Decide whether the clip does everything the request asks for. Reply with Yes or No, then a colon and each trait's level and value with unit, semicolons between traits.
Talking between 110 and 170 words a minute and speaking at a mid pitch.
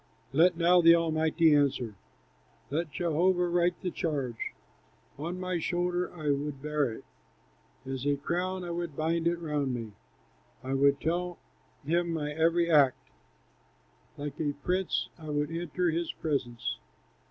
Yes: average, 140 wpm; medium, 160 Hz